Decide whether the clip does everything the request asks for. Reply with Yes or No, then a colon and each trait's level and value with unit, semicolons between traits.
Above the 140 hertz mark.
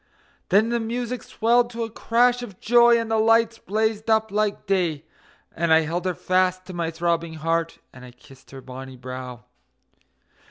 Yes: medium, 185 Hz